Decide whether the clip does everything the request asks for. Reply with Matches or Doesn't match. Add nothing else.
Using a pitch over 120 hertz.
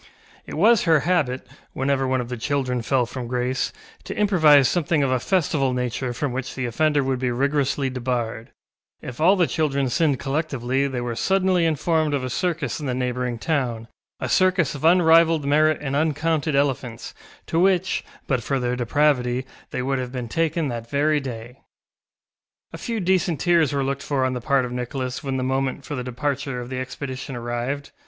Matches